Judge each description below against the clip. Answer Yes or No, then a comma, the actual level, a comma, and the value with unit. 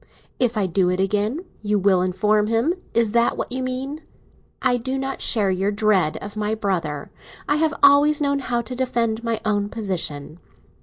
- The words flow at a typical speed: Yes, average, 185 wpm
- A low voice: No, high, 220 Hz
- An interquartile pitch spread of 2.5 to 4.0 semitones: No, average, 4.5 semitones